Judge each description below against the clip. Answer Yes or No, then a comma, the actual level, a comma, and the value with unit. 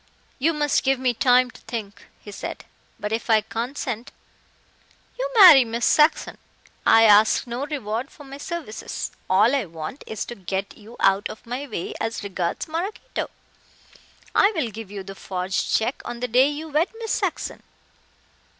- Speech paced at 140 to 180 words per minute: Yes, average, 170 wpm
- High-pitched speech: Yes, high, 240 Hz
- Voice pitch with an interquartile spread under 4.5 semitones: No, average, 5.3 semitones